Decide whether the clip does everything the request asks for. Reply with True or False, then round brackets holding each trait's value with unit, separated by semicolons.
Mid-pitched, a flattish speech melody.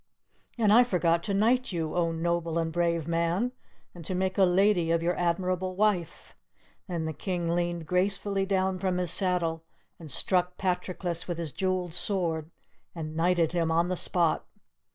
True (175 Hz; 2.0 semitones)